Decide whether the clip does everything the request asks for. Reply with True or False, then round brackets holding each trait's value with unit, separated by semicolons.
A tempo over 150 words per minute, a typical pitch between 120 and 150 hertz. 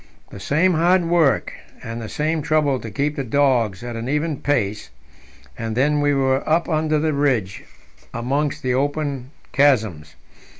True (160 wpm; 140 Hz)